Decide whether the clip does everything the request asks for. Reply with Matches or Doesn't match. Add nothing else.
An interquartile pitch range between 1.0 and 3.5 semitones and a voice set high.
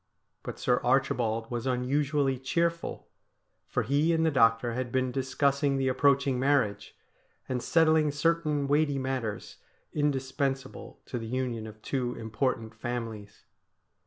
Doesn't match